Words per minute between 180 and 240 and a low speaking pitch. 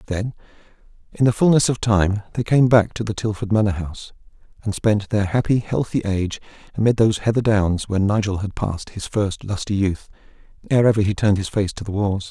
Yes: average, 200 wpm; low, 105 Hz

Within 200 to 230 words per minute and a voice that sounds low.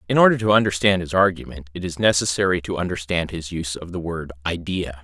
Yes: fast, 205 wpm; very low, 90 Hz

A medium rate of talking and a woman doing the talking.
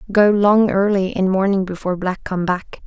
Yes: average, 190 wpm; female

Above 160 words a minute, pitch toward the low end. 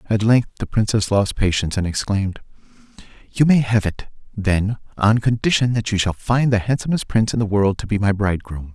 Yes: average, 200 wpm; low, 105 Hz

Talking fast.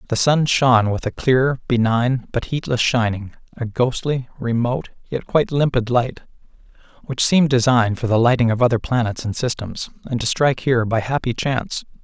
No: average, 175 wpm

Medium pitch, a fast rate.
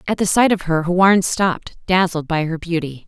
Yes: medium, 175 Hz; fast, 215 wpm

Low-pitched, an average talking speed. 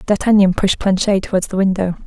No: high, 195 Hz; average, 175 wpm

